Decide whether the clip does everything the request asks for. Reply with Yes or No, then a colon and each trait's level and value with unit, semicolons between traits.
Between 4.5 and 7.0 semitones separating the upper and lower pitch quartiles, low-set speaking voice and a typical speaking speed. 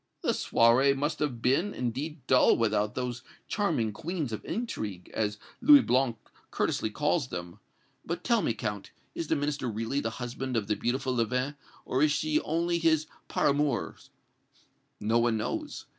Yes: average, 5.0 semitones; low, 130 Hz; average, 160 wpm